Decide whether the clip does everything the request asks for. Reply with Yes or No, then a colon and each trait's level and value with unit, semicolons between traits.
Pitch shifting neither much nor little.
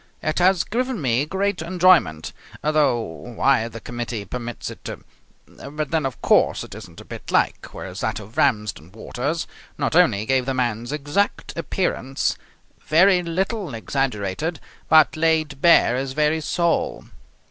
No: wide, 5.9 semitones